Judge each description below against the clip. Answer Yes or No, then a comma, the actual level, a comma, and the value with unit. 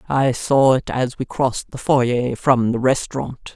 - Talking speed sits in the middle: Yes, average, 185 wpm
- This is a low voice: Yes, low, 130 Hz